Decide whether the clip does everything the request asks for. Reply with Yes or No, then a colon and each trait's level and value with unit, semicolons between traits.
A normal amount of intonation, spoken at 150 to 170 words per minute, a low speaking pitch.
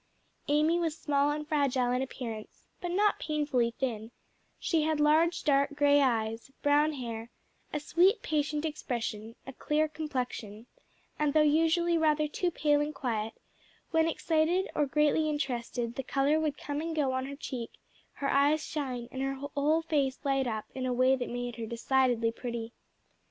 No: average, 3.7 semitones; average, 165 wpm; very high, 285 Hz